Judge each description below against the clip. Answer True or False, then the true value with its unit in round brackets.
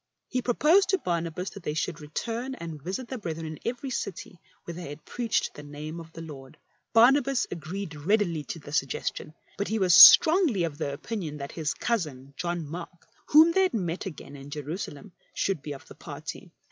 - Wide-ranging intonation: True (7.0 semitones)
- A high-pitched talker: False (170 Hz)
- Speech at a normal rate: True (195 wpm)